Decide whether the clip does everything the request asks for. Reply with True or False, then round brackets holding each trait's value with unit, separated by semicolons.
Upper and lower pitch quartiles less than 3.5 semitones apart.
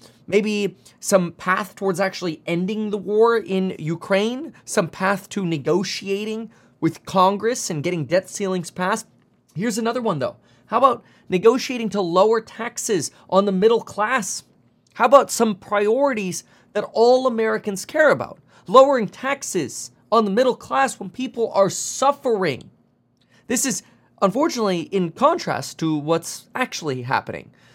False (4.0 semitones)